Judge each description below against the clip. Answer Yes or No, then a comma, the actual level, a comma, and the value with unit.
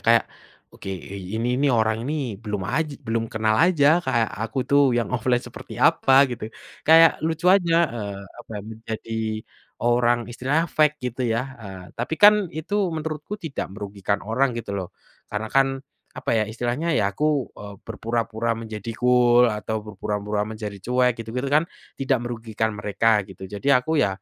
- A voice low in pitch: Yes, low, 115 Hz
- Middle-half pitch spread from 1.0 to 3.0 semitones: No, average, 3.9 semitones